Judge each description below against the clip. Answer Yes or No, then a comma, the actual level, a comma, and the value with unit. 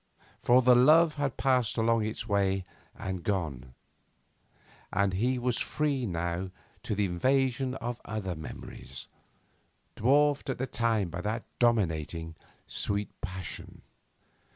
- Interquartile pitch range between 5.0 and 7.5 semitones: Yes, wide, 5.5 semitones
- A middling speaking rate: No, slow, 125 wpm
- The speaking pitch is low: Yes, low, 110 Hz